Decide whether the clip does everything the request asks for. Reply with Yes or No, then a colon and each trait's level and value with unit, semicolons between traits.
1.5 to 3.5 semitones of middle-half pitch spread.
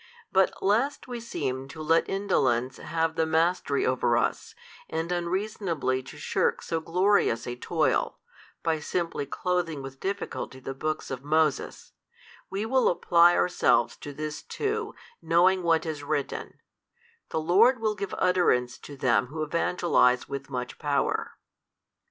No: average, 4.8 semitones